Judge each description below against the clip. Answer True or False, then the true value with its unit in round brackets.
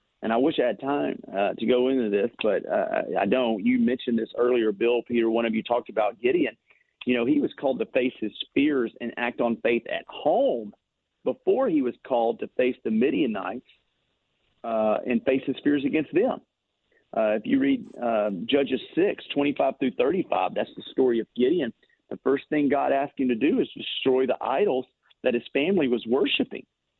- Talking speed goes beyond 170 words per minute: True (200 wpm)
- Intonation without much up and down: False (3.5 semitones)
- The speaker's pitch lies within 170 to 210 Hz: False (125 Hz)